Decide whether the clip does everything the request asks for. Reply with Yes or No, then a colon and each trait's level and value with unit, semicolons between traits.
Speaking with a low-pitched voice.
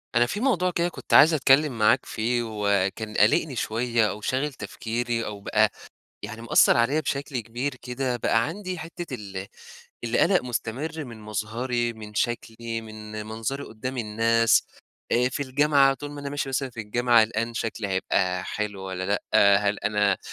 Yes: low, 115 Hz